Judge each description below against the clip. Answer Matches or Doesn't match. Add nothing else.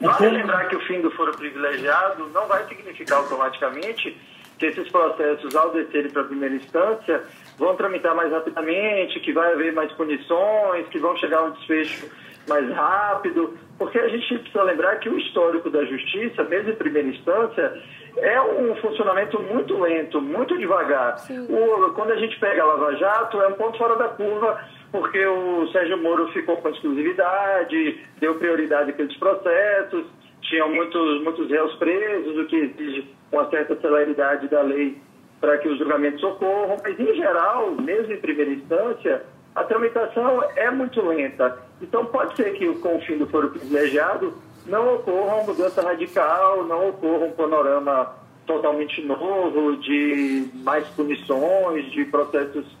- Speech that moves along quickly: Doesn't match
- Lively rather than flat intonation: Matches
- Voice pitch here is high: Doesn't match